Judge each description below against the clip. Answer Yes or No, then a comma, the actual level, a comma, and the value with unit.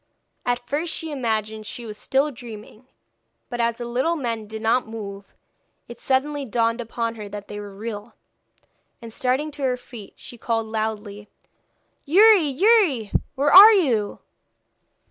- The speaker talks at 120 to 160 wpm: Yes, average, 150 wpm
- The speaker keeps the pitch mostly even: No, average, 4.1 semitones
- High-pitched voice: Yes, high, 235 Hz